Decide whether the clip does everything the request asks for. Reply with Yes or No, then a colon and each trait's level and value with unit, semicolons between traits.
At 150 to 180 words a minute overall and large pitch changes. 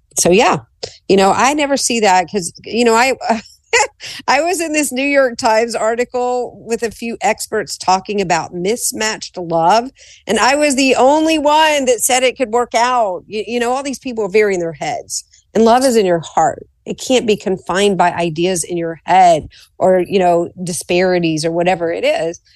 No: average, 195 wpm; wide, 5.7 semitones